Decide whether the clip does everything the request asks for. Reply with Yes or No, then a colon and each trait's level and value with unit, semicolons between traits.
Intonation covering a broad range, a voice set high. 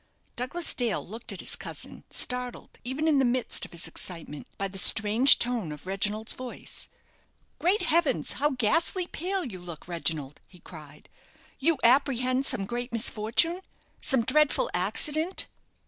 Yes: wide, 6.9 semitones; high, 245 Hz